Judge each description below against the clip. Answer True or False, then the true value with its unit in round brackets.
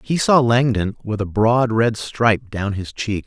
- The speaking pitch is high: False (110 Hz)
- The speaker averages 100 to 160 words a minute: False (200 wpm)